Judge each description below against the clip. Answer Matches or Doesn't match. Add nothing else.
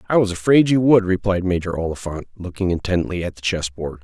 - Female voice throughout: Doesn't match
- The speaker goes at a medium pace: Doesn't match